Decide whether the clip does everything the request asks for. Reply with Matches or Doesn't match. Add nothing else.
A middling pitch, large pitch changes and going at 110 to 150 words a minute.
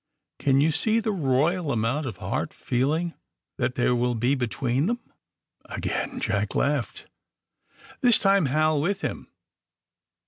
Matches